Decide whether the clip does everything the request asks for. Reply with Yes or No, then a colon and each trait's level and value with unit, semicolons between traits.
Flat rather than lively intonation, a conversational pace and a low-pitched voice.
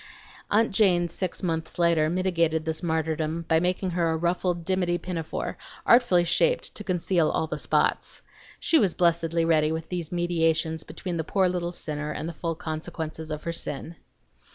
No: narrow, 1.9 semitones; average, 170 wpm; medium, 170 Hz